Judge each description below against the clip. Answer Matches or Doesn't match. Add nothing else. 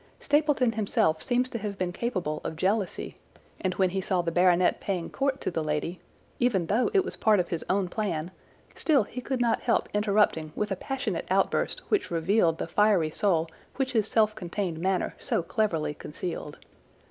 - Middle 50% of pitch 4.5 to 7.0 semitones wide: Matches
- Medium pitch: Doesn't match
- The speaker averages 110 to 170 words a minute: Doesn't match